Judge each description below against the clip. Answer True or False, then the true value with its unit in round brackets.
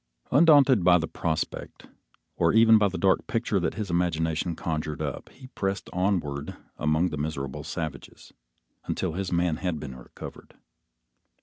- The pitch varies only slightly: False (4.1 semitones)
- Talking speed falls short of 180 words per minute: True (145 wpm)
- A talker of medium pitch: False (85 Hz)